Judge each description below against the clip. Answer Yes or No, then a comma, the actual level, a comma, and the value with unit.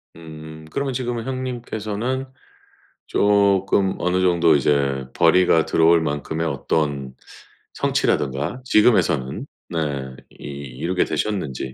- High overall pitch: No, very low, 85 Hz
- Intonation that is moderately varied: No, wide, 6.2 semitones